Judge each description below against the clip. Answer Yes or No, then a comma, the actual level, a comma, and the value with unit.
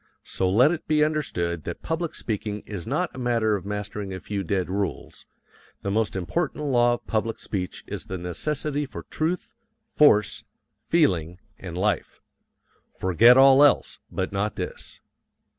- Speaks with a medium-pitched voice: No, low, 105 Hz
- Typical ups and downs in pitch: No, wide, 7.2 semitones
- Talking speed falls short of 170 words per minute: Yes, average, 155 wpm